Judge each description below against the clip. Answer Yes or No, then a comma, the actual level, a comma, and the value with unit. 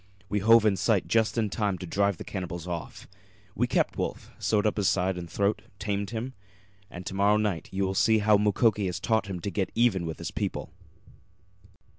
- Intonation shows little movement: Yes, narrow, 2.3 semitones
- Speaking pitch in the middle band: No, low, 100 Hz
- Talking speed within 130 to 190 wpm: No, fast, 205 wpm